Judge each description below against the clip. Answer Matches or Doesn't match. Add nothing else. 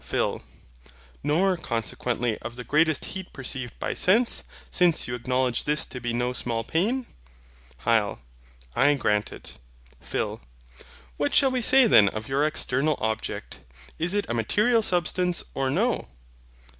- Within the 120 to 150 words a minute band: Matches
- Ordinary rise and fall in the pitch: Doesn't match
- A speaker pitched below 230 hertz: Matches